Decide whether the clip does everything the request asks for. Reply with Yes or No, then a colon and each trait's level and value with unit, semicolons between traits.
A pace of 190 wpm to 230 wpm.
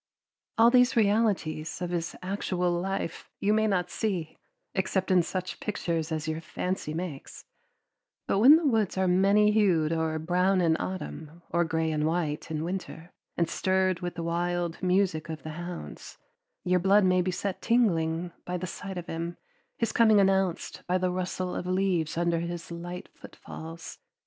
No: average, 170 wpm